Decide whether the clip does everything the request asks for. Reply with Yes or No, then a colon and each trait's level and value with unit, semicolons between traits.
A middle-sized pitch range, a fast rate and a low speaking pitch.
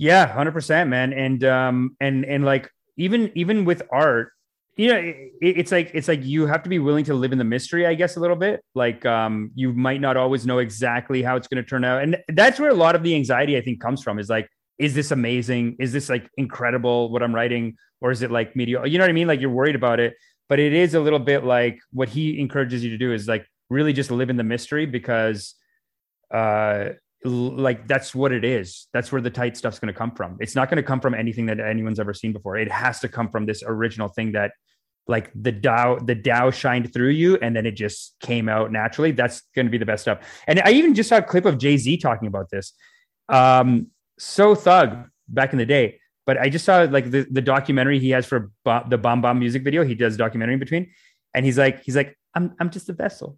Yes: average, 4.0 semitones; fast, 245 wpm; low, 130 Hz